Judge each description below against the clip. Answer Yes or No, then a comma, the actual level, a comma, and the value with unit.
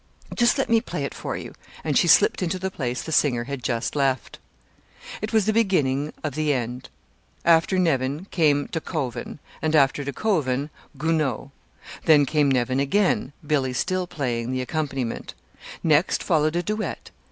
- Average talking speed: Yes, average, 165 wpm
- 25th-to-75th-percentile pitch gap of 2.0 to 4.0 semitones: No, average, 4.8 semitones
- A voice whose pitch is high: No, medium, 150 Hz